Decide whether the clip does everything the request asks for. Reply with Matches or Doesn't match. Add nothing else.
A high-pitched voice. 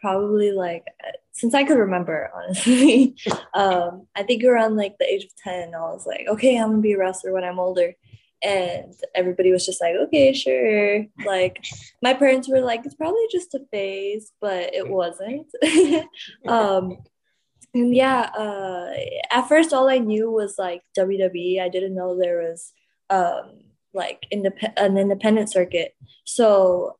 Matches